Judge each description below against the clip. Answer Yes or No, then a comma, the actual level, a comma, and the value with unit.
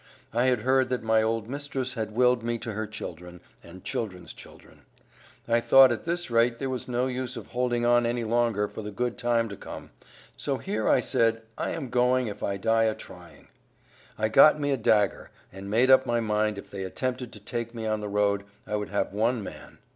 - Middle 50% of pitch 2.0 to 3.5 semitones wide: Yes, average, 2.8 semitones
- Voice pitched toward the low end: Yes, low, 115 Hz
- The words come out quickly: Yes, fast, 215 wpm